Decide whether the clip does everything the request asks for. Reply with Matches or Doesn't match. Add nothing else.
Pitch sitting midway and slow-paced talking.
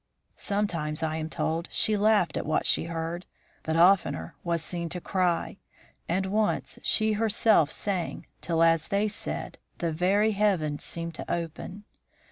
Doesn't match